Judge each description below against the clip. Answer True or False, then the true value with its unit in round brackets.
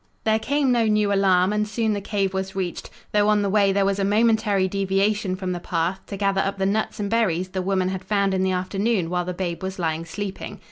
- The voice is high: True (195 Hz)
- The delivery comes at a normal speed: False (240 wpm)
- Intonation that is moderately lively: False (2.0 semitones)